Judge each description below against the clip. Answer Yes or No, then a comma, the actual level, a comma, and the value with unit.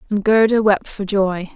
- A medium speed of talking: Yes, average, 190 wpm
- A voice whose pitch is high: Yes, high, 200 Hz